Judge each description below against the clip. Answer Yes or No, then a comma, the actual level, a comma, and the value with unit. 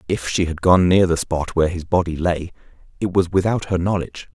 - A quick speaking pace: Yes, fast, 220 wpm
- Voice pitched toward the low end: Yes, very low, 90 Hz